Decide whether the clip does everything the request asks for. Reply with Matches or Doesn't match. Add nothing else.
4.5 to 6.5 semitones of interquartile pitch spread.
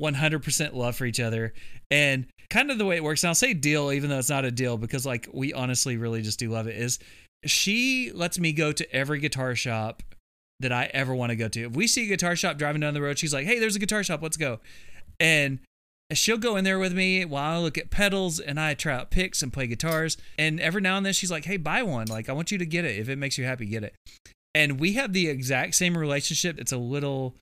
Matches